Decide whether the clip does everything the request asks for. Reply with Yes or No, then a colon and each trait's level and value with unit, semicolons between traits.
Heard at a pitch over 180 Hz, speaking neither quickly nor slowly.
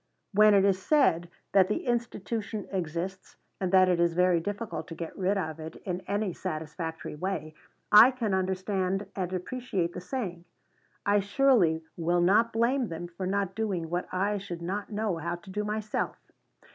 Yes: high, 190 Hz; average, 170 wpm